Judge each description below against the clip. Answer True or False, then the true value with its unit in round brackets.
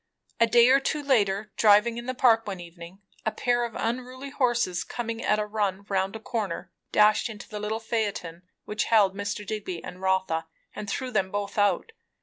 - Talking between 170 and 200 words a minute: True (190 wpm)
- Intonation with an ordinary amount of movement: True (3.3 semitones)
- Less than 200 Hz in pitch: False (210 Hz)